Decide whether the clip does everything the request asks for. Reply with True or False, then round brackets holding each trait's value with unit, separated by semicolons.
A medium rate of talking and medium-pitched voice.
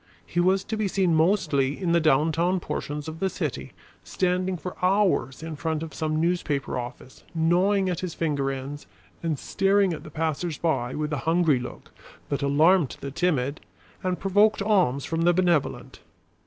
True (170 wpm; 165 Hz)